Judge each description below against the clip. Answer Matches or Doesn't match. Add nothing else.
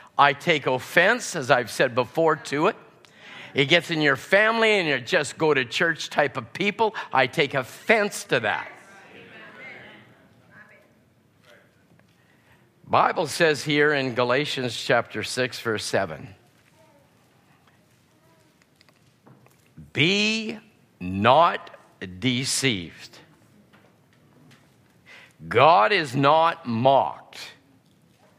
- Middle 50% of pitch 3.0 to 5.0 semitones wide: Doesn't match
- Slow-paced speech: Matches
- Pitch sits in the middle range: Matches